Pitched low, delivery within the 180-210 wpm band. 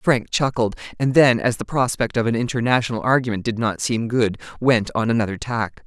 Yes: low, 115 Hz; average, 195 wpm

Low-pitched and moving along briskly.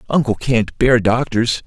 No: low, 120 Hz; average, 145 wpm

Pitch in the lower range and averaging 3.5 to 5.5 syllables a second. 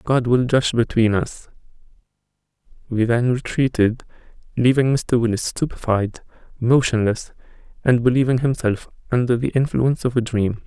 Yes: low, 120 Hz; 5.1 syllables/s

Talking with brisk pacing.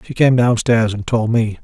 Yes: fast, 220 wpm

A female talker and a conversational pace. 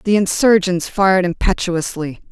No: female; slow, 105 wpm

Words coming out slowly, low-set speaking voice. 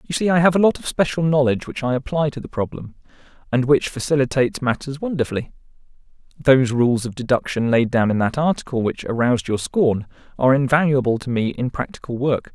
No: average, 190 wpm; low, 130 Hz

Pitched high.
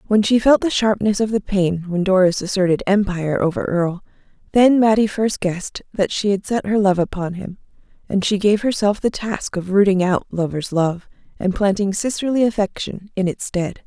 Yes: high, 195 Hz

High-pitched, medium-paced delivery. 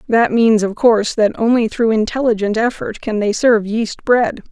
Yes: high, 225 Hz; average, 185 wpm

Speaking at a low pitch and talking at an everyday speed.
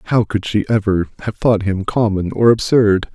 Yes: low, 105 Hz; average, 190 wpm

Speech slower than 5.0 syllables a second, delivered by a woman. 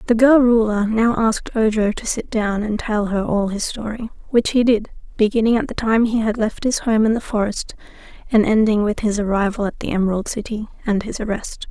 No: 5.4 syllables/s; female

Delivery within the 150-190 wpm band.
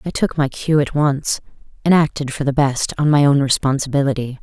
No: fast, 205 wpm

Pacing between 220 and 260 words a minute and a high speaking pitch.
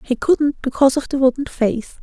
No: fast, 205 wpm; very high, 265 Hz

